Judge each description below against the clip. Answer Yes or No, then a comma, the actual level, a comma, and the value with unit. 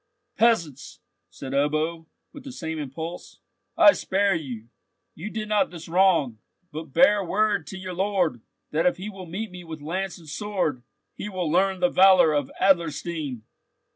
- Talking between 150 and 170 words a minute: Yes, average, 165 wpm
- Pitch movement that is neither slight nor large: Yes, average, 3.9 semitones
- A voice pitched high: No, medium, 175 Hz